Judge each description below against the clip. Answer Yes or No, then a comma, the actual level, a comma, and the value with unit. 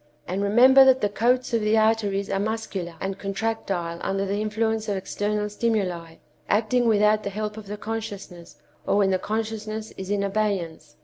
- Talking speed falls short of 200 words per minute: Yes, average, 175 wpm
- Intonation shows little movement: Yes, narrow, 2.2 semitones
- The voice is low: No, high, 210 Hz